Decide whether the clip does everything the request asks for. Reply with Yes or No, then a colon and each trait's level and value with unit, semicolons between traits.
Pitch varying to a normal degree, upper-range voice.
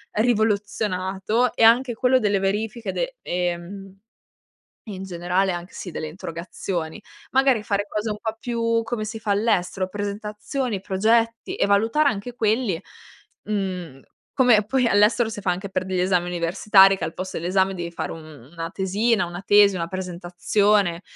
Yes: average, 3.5 semitones; high, 200 Hz